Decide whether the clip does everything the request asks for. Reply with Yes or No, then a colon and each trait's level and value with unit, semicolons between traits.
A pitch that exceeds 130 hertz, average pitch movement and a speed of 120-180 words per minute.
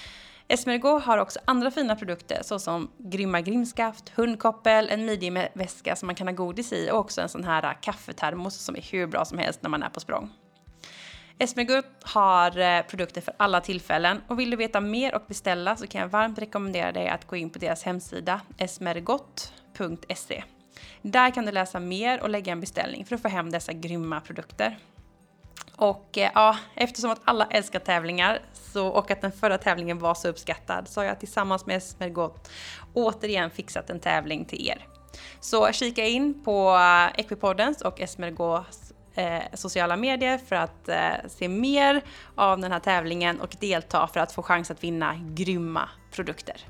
Yes: high, 190 Hz; average, 4.1 semitones; average, 170 wpm